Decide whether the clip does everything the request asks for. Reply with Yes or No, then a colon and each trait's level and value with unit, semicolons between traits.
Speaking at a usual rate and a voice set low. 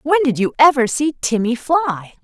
No: average, 190 wpm; very high, 265 Hz